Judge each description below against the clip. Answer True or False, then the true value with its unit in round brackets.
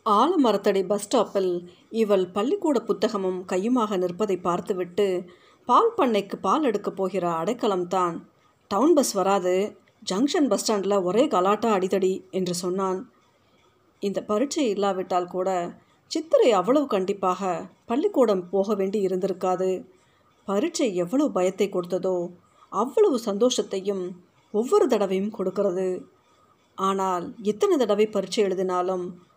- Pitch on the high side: True (195 Hz)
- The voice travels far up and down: False (2.7 semitones)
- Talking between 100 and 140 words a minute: True (105 wpm)